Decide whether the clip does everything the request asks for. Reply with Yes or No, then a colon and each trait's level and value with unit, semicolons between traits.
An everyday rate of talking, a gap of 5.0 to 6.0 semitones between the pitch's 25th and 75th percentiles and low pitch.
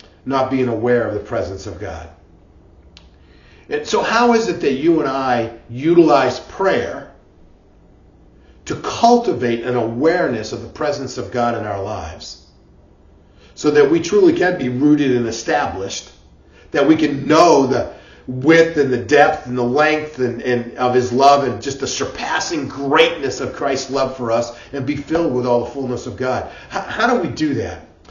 Yes: average, 175 wpm; wide, 5.6 semitones; low, 125 Hz